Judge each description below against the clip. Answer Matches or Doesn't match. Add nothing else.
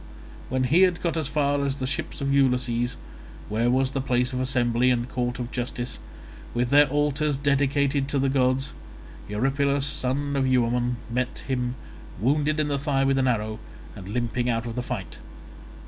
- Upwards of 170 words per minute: Matches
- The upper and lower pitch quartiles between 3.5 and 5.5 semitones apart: Doesn't match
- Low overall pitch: Matches